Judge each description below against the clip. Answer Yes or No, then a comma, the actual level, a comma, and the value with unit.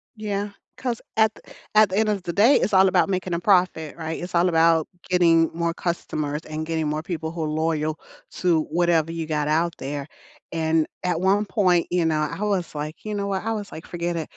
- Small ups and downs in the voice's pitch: No, average, 3.1 semitones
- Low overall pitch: No, medium, 170 Hz